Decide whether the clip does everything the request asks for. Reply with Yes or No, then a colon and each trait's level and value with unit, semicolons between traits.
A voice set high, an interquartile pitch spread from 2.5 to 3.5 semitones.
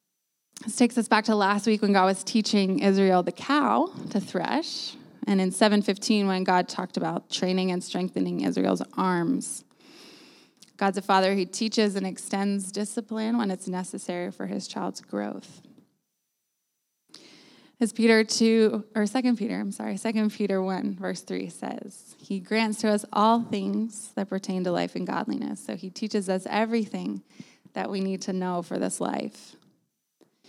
Yes: high, 200 Hz; average, 3.0 semitones